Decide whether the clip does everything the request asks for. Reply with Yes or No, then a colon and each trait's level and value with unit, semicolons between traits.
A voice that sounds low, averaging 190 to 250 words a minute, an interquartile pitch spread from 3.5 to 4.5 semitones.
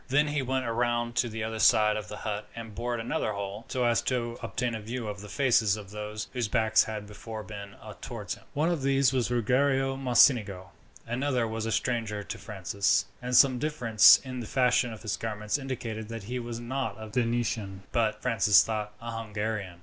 No: low, 115 Hz; average, 200 wpm; average, 2.8 semitones